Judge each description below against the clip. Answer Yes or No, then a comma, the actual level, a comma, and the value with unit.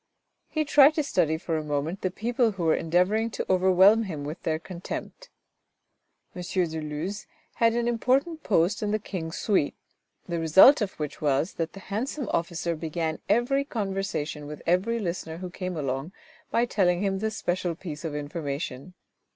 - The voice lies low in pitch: No, medium, 180 Hz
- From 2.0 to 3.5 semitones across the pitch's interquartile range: No, average, 5.1 semitones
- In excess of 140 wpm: Yes, average, 170 wpm